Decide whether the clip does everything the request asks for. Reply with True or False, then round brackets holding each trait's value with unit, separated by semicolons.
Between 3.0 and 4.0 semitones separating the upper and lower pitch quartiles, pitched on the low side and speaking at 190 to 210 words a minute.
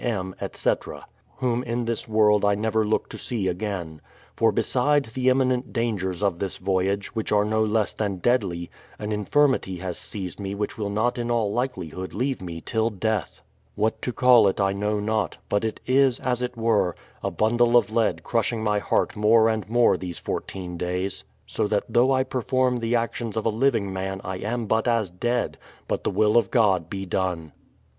True (3.6 semitones; 110 Hz; 195 wpm)